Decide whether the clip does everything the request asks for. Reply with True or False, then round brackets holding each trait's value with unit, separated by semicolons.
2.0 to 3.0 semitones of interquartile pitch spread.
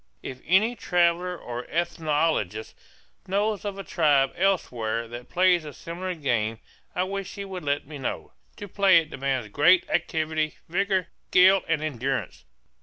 False (5.4 semitones)